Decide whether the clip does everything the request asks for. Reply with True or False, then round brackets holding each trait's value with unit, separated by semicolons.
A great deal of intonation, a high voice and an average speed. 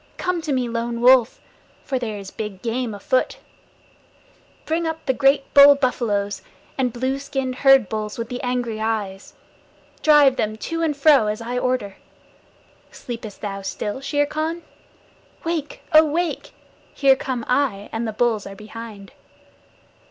False (4.5 semitones; 250 Hz; 150 wpm)